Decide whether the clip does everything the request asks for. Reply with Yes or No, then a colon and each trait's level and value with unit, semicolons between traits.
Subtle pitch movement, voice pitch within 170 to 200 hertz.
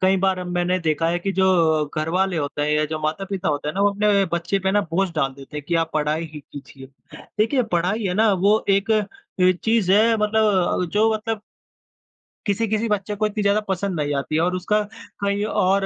No: average, 4.0 semitones; high, 190 Hz